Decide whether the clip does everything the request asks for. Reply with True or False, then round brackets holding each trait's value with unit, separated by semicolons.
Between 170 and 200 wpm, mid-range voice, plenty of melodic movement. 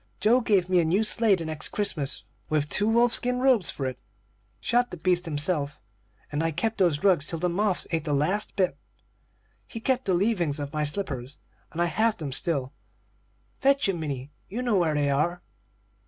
True (195 wpm; 175 Hz; 6.0 semitones)